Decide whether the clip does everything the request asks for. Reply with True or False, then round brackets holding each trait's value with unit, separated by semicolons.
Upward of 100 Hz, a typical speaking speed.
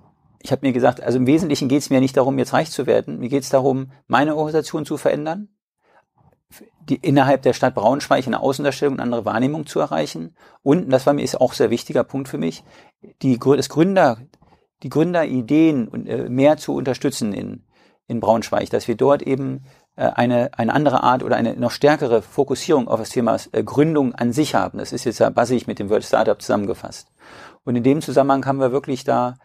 False (135 Hz; 210 wpm)